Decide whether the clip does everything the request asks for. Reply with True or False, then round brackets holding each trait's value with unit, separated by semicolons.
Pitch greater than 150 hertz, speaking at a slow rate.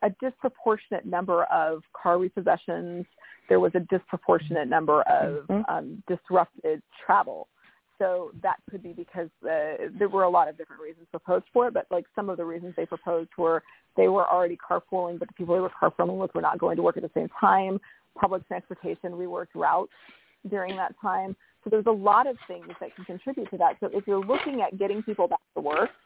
False (185 Hz; 205 wpm)